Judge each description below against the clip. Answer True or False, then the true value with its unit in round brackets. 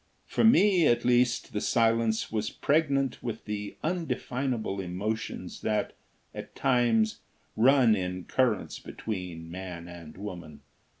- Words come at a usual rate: False (120 wpm)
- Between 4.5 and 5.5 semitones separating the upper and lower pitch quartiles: True (4.9 semitones)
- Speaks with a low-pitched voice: True (110 Hz)